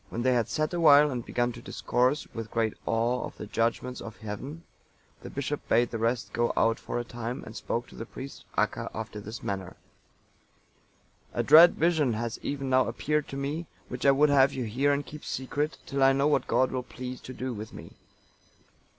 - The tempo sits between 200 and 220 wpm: Yes, fast, 205 wpm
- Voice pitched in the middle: No, low, 125 Hz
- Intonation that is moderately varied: Yes, average, 3.5 semitones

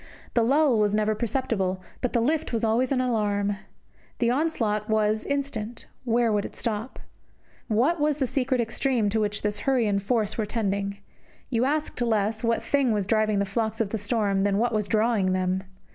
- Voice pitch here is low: No, high, 220 Hz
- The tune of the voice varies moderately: Yes, average, 3.0 semitones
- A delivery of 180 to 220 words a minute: Yes, average, 190 wpm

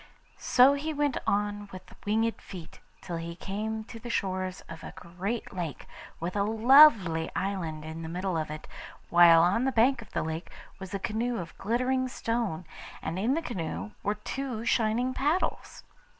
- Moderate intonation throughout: No, wide, 5.7 semitones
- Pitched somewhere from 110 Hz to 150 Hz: No, high, 205 Hz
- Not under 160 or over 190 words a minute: Yes, average, 175 wpm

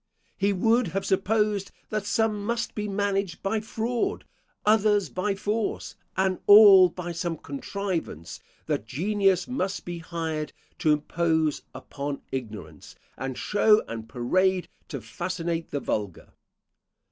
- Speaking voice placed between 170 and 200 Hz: Yes, medium, 185 Hz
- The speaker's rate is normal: No, slow, 125 wpm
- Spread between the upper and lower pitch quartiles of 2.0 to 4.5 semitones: No, average, 5.0 semitones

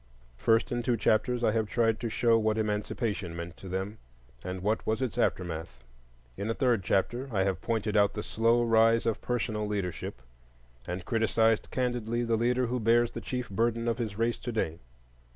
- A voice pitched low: Yes, low, 110 Hz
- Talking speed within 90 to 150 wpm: No, average, 190 wpm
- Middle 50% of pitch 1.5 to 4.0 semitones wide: Yes, narrow, 2.5 semitones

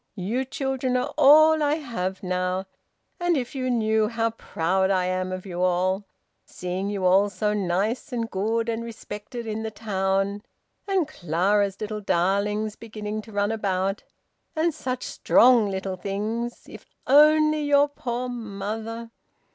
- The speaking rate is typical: Yes, average, 145 wpm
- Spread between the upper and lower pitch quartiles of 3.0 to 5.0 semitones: Yes, average, 4.3 semitones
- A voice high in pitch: Yes, high, 215 Hz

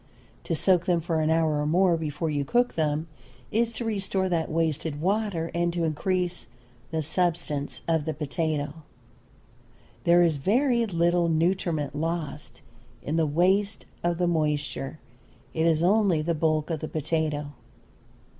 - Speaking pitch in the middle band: Yes, medium, 165 Hz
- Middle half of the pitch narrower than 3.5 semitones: Yes, narrow, 2.5 semitones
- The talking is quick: No, average, 150 wpm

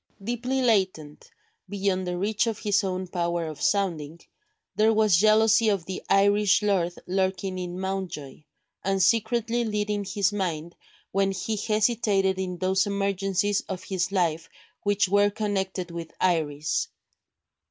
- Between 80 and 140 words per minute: Yes, slow, 135 wpm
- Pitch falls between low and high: No, high, 195 Hz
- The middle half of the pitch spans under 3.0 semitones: Yes, narrow, 2.5 semitones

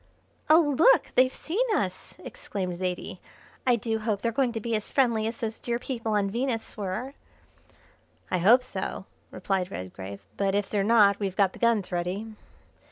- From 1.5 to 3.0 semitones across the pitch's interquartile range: No, average, 3.6 semitones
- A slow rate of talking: No, average, 170 wpm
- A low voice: No, high, 215 Hz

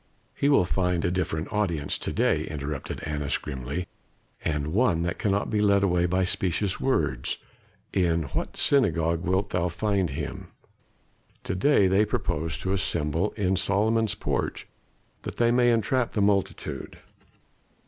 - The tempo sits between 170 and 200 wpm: No, average, 145 wpm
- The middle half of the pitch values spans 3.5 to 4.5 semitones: Yes, average, 4.0 semitones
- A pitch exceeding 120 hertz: No, very low, 90 Hz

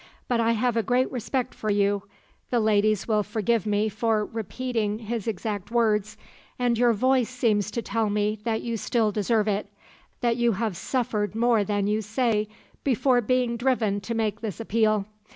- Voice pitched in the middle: No, high, 220 Hz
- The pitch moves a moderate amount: No, narrow, 2.2 semitones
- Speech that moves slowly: No, average, 175 wpm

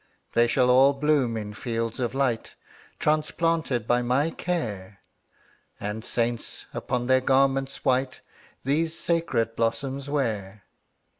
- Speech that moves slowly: Yes, slow, 120 wpm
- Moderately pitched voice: No, low, 130 Hz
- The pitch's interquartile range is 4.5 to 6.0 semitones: No, average, 3.3 semitones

